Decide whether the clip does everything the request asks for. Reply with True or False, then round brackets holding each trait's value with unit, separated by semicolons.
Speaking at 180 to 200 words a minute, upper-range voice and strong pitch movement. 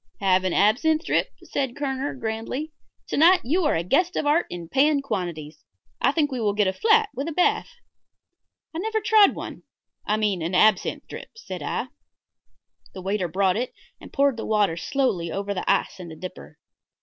True (190 wpm; 225 Hz; 8.0 semitones)